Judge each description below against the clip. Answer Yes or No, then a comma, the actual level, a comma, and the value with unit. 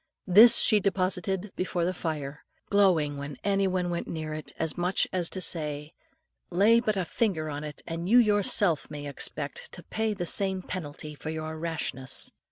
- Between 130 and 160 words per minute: No, average, 175 wpm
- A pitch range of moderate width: Yes, average, 4.0 semitones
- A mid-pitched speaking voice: Yes, medium, 175 Hz